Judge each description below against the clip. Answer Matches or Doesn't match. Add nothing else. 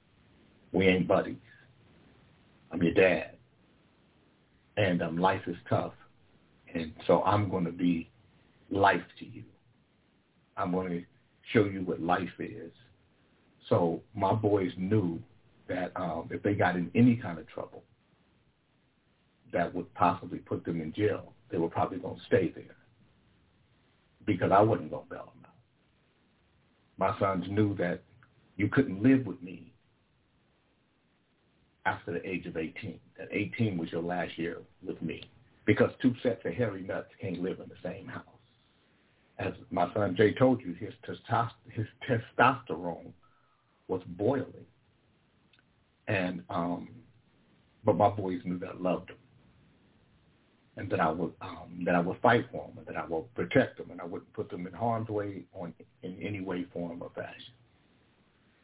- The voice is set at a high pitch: Doesn't match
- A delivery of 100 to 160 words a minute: Matches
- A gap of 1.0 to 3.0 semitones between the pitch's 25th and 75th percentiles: Doesn't match